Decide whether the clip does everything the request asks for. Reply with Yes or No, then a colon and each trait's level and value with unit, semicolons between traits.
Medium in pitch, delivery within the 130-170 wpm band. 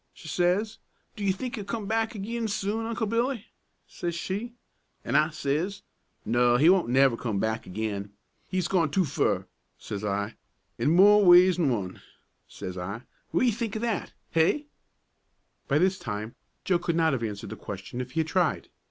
No: medium, 170 Hz; average, 180 wpm